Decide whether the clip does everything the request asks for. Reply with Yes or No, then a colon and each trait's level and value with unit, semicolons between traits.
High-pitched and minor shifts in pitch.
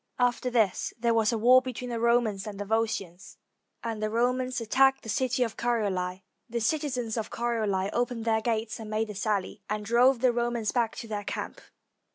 Yes: high, 230 Hz; narrow, 2.3 semitones